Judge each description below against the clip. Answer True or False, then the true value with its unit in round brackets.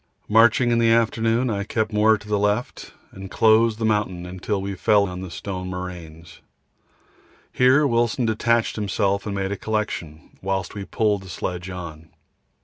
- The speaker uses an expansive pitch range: False (3.3 semitones)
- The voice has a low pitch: True (105 Hz)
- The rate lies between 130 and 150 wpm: False (165 wpm)